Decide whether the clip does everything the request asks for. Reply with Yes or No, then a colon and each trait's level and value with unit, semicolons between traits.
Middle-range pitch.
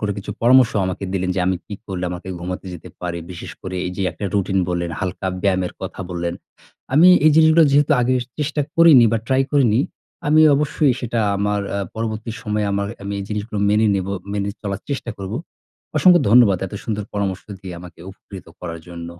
No: low, 100 Hz